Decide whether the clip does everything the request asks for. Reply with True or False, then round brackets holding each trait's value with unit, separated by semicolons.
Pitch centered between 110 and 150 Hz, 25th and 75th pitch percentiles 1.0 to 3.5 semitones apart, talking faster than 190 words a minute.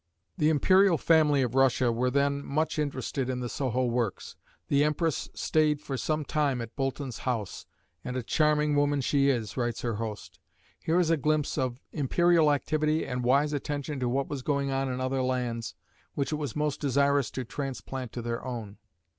False (140 Hz; 3.1 semitones; 185 wpm)